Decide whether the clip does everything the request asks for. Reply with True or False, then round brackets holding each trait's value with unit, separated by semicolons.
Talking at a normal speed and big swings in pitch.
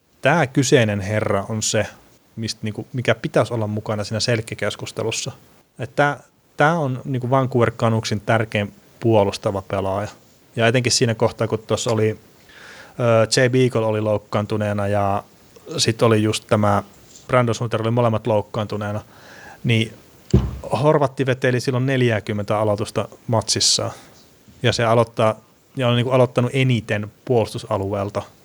False (110 wpm; 2.8 semitones)